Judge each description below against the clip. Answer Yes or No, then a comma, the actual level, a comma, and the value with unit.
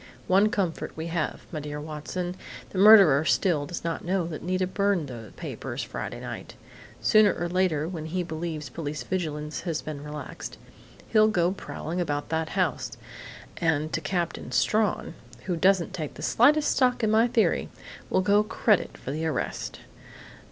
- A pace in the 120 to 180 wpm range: Yes, average, 165 wpm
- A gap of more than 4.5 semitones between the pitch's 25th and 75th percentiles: No, average, 4.1 semitones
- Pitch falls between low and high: Yes, medium, 170 Hz